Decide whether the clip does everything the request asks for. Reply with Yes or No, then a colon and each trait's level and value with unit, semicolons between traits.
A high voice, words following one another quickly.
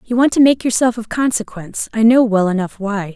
Yes: high, 225 Hz; fast, 230 wpm